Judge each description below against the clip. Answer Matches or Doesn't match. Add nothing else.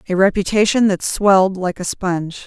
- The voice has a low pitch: Doesn't match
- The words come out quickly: Doesn't match